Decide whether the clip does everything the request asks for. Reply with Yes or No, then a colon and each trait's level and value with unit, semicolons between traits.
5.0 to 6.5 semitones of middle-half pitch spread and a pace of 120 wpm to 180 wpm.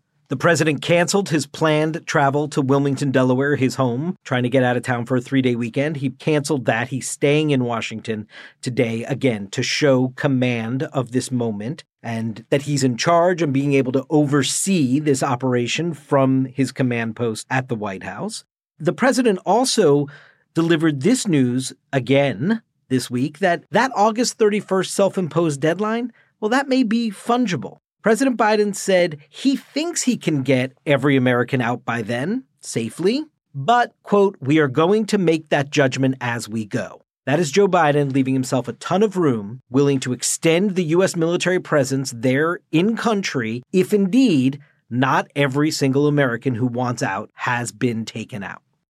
Yes: wide, 5.4 semitones; average, 165 wpm